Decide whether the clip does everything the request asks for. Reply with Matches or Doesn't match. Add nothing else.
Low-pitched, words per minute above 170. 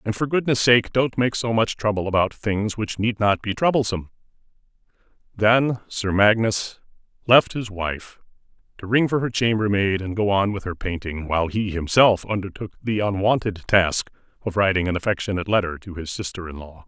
Matches